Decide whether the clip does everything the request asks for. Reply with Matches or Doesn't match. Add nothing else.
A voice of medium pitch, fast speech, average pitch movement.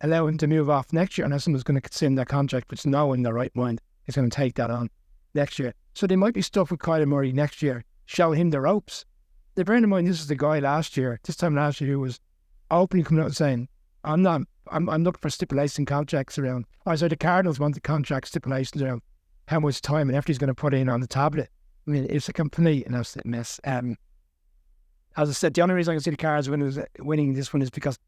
Matches